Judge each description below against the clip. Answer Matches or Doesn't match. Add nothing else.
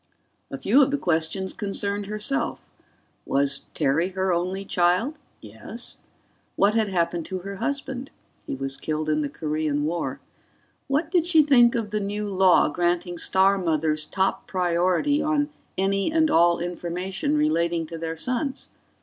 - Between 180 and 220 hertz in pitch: Matches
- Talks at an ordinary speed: Matches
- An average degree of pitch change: Doesn't match